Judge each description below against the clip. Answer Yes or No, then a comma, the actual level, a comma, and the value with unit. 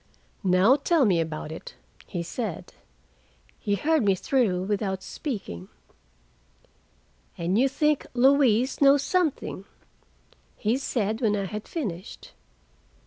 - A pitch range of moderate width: No, wide, 6.3 semitones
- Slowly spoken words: Yes, slow, 115 wpm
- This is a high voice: Yes, high, 215 Hz